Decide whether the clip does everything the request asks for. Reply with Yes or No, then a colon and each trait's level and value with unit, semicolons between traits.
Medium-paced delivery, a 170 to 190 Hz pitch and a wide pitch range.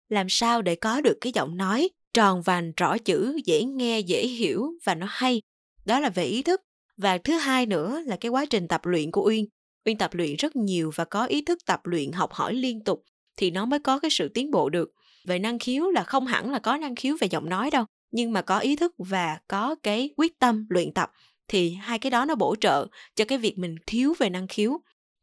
No: average, 240 wpm; high, 225 Hz; wide, 6.1 semitones